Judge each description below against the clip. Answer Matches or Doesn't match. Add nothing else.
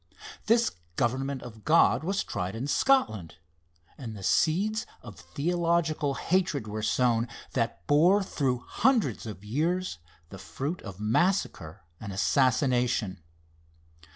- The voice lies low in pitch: Matches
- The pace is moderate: Doesn't match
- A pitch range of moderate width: Doesn't match